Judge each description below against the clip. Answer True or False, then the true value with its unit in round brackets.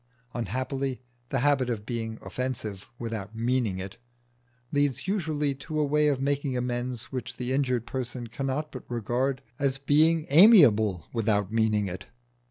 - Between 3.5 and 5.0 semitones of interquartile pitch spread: True (3.8 semitones)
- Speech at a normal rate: True (150 wpm)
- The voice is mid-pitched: False (125 Hz)